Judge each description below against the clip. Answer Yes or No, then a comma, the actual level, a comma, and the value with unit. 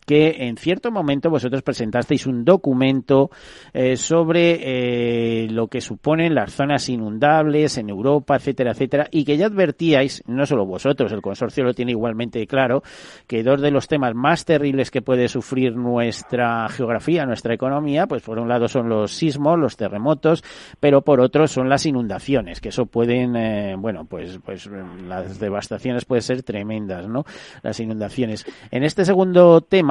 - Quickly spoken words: No, average, 165 wpm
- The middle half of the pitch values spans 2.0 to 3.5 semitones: No, average, 4.1 semitones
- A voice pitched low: Yes, low, 130 Hz